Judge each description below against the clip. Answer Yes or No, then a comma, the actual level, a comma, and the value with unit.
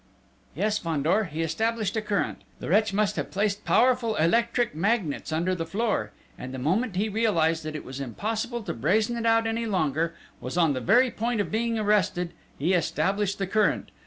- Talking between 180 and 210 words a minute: Yes, average, 190 wpm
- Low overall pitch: No, high, 200 Hz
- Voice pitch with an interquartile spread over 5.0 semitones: Yes, wide, 5.5 semitones